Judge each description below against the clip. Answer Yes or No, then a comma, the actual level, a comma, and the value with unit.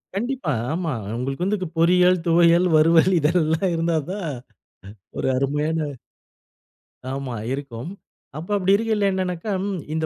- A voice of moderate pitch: Yes, medium, 170 Hz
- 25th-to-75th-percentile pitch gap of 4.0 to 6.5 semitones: No, average, 3.5 semitones